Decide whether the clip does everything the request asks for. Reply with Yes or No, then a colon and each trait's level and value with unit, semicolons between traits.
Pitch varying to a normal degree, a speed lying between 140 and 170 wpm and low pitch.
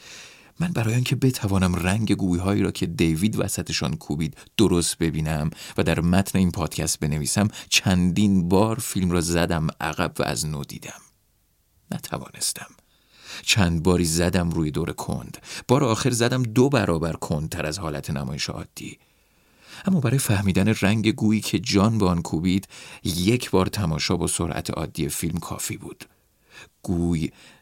Yes: average, 4.3 semitones; average, 150 wpm; very low, 95 Hz